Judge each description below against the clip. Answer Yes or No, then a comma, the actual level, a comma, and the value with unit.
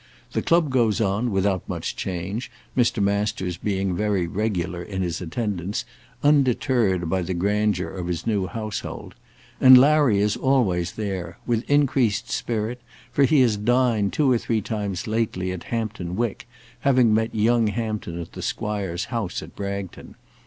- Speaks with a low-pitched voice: Yes, low, 105 Hz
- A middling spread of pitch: Yes, average, 4.0 semitones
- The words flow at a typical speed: Yes, average, 155 wpm